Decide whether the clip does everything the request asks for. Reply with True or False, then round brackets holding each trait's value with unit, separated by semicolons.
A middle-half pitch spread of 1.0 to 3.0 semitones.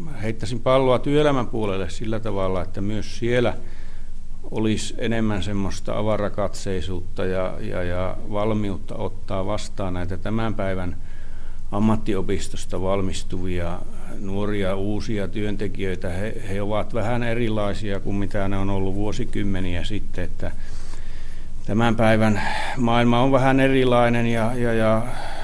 True (2.7 semitones)